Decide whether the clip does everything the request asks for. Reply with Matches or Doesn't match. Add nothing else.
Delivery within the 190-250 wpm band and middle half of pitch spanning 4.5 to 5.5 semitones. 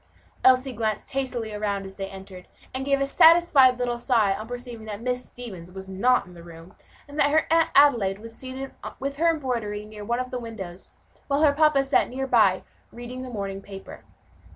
Matches